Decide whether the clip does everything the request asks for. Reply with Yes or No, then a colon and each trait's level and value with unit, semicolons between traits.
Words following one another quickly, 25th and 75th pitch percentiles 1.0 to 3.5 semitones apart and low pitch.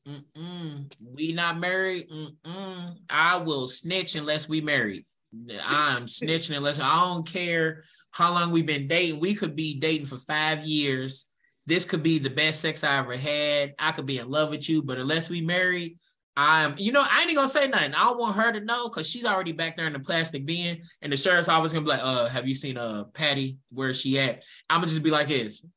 No: fast, 225 wpm; average, 3.2 semitones; medium, 160 Hz